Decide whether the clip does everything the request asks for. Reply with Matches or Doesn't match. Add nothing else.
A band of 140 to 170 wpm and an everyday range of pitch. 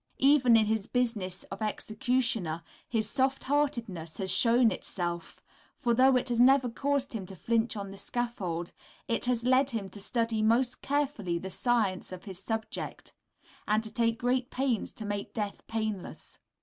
Matches